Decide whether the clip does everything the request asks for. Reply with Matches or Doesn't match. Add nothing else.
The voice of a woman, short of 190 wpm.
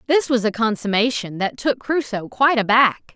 Matches